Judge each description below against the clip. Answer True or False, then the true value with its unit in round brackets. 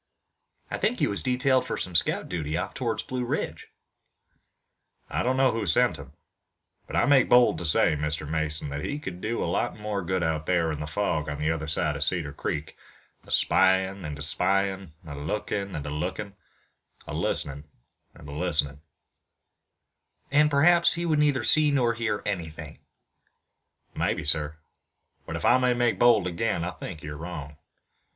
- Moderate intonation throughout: False (7.4 semitones)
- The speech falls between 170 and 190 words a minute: True (180 wpm)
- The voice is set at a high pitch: False (90 Hz)